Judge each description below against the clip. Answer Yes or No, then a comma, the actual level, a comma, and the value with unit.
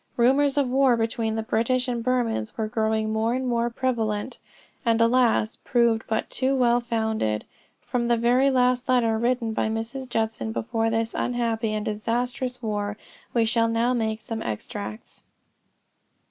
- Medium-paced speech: Yes, average, 160 wpm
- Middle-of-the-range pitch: No, high, 230 Hz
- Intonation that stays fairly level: Yes, narrow, 2.1 semitones